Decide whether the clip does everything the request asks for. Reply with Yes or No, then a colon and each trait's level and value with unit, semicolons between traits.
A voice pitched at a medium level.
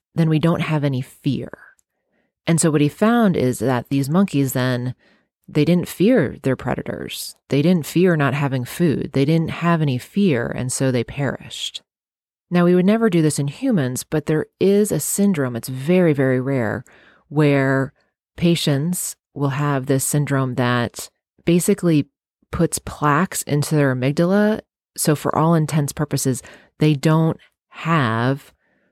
Yes: medium, 145 Hz